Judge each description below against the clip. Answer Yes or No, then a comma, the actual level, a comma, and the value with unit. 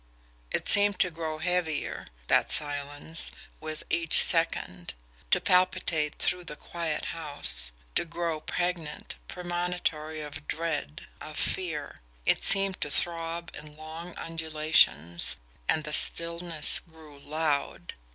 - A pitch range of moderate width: No, narrow, 2.3 semitones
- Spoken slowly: Yes, slow, 120 wpm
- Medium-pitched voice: Yes, medium, 160 Hz